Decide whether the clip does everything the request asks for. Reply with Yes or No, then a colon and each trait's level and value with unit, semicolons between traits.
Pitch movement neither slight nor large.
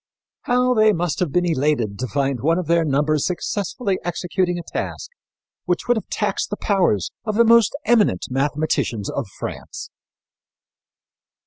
No: wide, 6.3 semitones